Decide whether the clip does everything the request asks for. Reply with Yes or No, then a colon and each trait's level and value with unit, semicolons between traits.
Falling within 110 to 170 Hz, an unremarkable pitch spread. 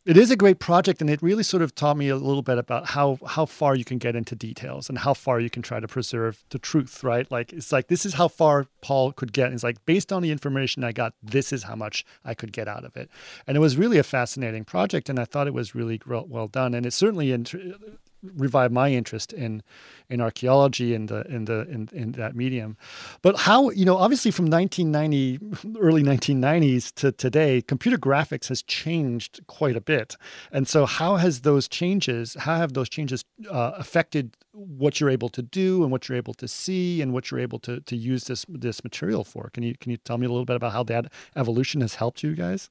Yes: low, 135 Hz; average, 4.7 semitones